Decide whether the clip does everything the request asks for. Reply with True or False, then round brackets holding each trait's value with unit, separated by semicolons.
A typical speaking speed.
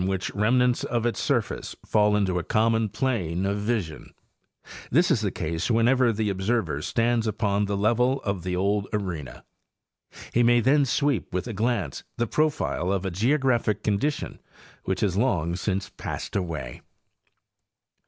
True (155 wpm)